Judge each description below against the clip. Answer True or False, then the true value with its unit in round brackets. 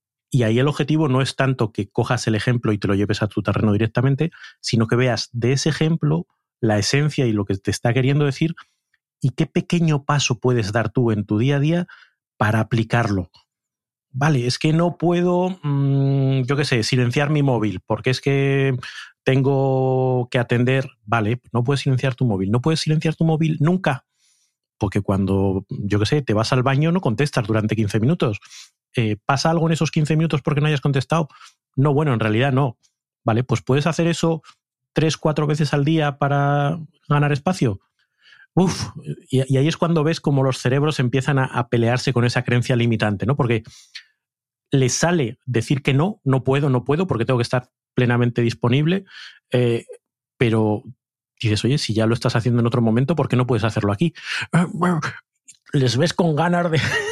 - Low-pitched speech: True (130 Hz)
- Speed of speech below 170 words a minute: False (185 wpm)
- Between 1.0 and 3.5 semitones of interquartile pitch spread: False (4.3 semitones)